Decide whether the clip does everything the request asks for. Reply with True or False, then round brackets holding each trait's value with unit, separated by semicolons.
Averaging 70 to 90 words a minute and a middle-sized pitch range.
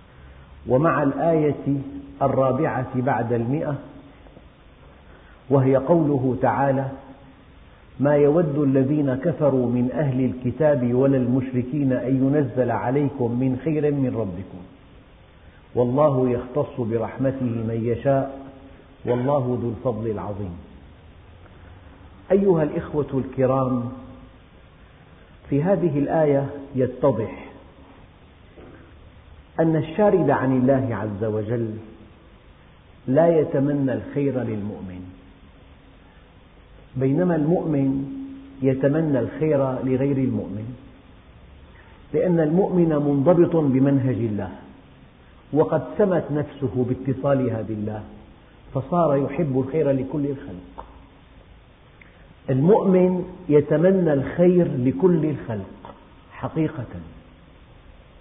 False (80 wpm; 5.8 semitones)